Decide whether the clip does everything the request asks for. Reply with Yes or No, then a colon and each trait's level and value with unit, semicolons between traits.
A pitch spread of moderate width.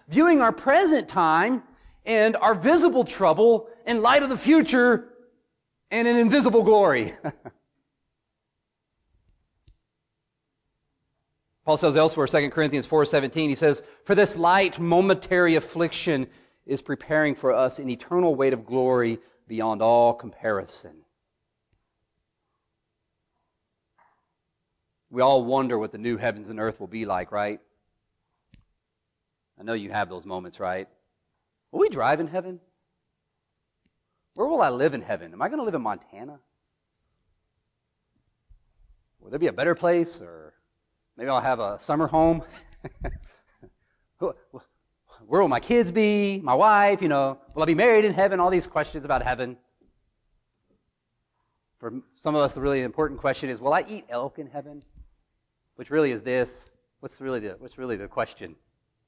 No: wide, 7.7 semitones